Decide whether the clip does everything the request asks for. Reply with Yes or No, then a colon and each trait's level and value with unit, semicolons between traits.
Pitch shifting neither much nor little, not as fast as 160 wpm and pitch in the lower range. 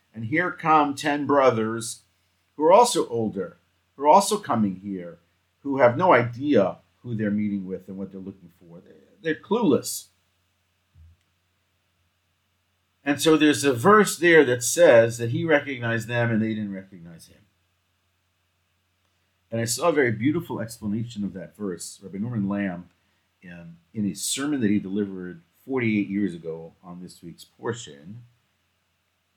Yes: average, 4.4 semitones; average, 150 wpm; low, 100 Hz